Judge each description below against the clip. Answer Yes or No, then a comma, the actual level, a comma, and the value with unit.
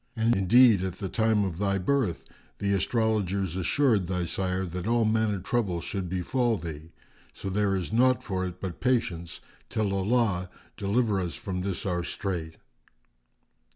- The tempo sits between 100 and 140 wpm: No, average, 155 wpm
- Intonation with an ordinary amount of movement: Yes, average, 3.5 semitones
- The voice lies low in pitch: Yes, very low, 95 Hz